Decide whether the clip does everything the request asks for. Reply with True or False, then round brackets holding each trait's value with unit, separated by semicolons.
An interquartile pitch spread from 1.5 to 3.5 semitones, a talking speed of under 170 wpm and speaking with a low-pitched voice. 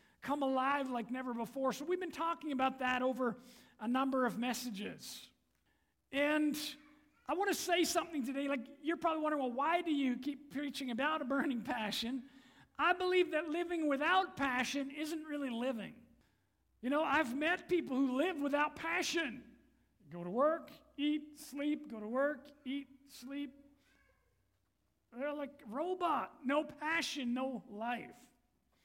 False (2.8 semitones; 155 wpm; 280 Hz)